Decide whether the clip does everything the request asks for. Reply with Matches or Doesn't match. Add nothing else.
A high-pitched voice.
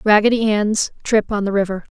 Matches